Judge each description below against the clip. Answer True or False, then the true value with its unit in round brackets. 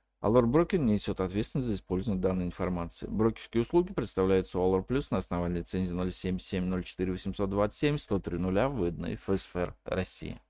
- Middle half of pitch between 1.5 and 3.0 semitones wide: False (3.4 semitones)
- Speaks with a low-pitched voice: True (95 Hz)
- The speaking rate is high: False (120 wpm)